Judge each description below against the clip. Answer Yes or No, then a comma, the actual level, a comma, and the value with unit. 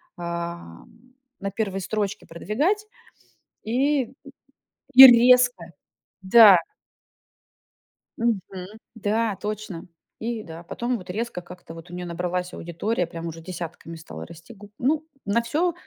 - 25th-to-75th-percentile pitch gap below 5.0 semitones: No, wide, 5.5 semitones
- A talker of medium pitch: No, high, 200 Hz